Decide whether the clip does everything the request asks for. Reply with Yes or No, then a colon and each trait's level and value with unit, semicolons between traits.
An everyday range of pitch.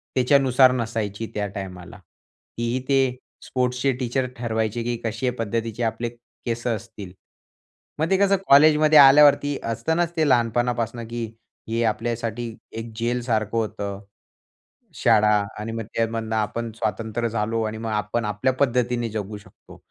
No: narrow, 2.2 semitones